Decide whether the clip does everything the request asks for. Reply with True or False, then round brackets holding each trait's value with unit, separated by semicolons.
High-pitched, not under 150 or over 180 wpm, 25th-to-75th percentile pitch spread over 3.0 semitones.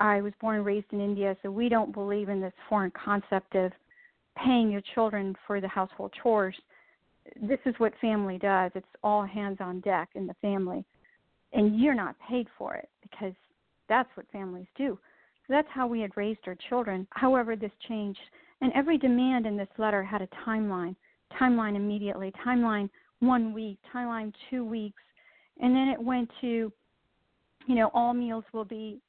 True (215 Hz; 175 wpm; 3.7 semitones)